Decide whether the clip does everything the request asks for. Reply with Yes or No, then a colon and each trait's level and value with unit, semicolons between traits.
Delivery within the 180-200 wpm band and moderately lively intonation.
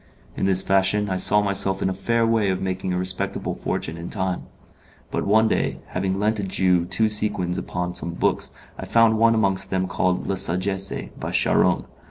No: average, 195 wpm; narrow, 2.2 semitones